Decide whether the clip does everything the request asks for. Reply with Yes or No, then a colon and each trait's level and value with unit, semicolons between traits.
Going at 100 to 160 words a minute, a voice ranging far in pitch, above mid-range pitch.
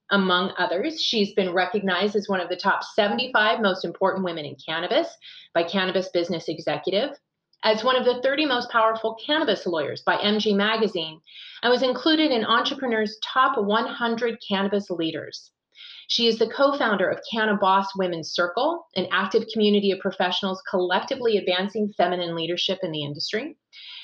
No: average, 155 wpm; average, 4.1 semitones; high, 205 Hz